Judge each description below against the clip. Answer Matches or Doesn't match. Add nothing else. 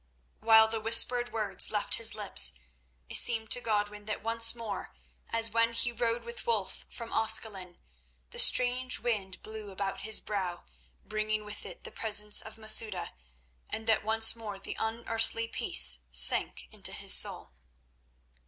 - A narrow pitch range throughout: Matches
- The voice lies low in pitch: Doesn't match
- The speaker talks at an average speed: Matches